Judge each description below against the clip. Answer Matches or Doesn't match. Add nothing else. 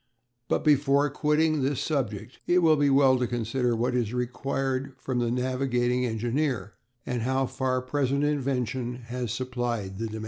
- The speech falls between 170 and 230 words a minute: Doesn't match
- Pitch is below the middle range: Matches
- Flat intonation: Matches